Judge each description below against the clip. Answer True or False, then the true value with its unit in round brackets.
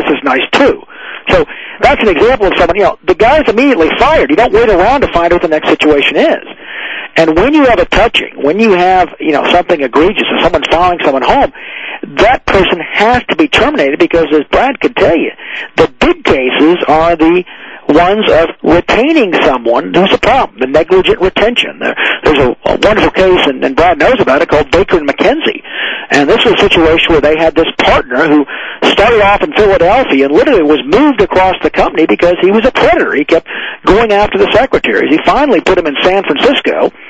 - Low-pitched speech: False (180 Hz)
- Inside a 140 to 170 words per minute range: False (205 wpm)